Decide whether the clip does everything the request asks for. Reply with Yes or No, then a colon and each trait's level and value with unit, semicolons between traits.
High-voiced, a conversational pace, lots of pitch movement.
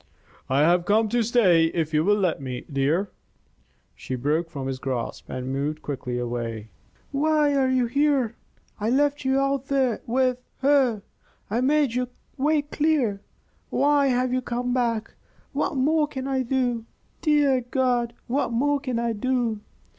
Yes: high, 245 Hz; average, 160 wpm; wide, 7.9 semitones